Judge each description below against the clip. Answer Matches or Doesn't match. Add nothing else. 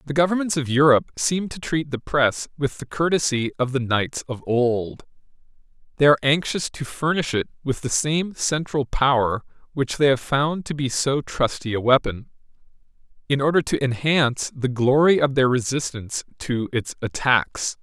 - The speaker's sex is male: Matches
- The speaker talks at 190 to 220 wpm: Doesn't match